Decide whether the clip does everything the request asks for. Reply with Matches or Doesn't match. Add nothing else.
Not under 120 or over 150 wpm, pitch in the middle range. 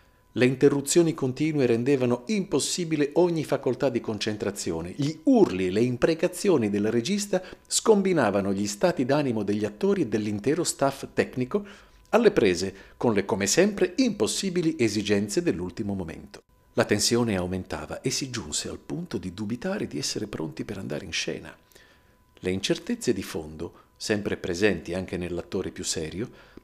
Doesn't match